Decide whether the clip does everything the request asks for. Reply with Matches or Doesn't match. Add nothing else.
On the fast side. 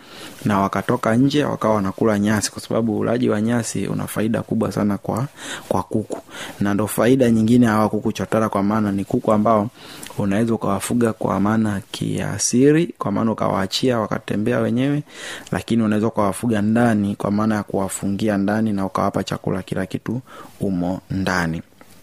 Matches